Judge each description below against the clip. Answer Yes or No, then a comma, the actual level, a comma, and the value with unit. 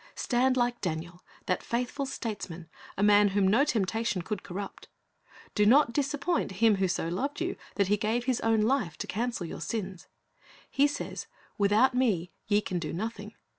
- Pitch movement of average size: Yes, average, 4.5 semitones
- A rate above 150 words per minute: Yes, average, 170 wpm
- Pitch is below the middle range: No, high, 215 Hz